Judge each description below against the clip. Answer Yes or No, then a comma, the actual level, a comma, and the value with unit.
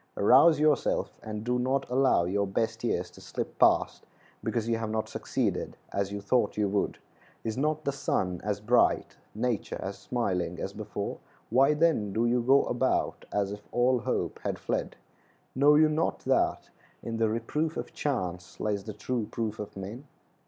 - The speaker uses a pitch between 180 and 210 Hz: No, low, 115 Hz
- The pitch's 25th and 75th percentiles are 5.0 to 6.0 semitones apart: No, average, 4.4 semitones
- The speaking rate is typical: Yes, average, 175 wpm